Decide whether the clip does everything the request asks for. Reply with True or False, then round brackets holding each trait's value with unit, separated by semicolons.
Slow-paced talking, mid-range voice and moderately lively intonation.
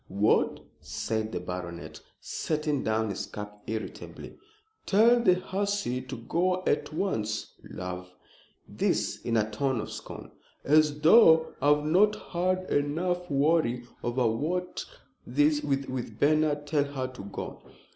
False (125 wpm; 145 Hz; 6.8 semitones)